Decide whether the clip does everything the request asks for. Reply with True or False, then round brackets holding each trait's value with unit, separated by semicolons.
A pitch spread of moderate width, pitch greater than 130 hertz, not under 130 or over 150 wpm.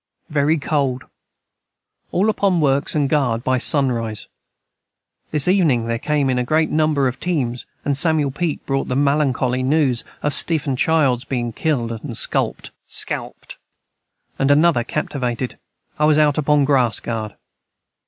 True (3.5 semitones; 140 Hz; 145 wpm)